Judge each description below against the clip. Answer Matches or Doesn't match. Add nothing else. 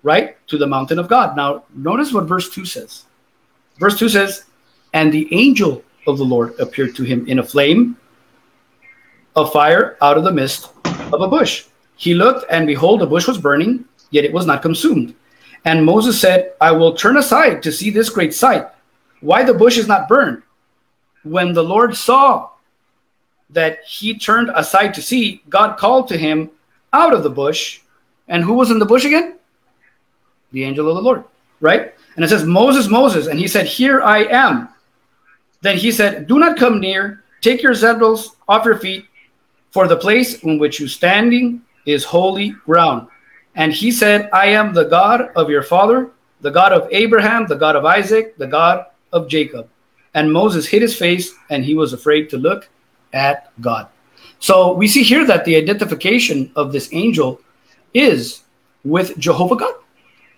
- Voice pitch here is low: Doesn't match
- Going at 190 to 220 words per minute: Doesn't match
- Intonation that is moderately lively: Doesn't match